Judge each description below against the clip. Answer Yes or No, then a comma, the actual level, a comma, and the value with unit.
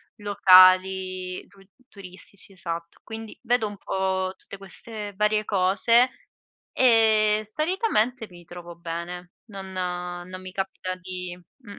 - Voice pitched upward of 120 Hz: Yes, high, 190 Hz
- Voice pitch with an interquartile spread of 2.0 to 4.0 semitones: Yes, average, 2.7 semitones